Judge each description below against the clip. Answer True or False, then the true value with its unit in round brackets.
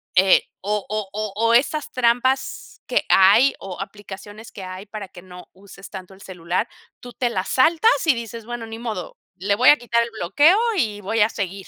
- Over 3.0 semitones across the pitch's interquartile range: True (3.8 semitones)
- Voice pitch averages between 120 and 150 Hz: False (215 Hz)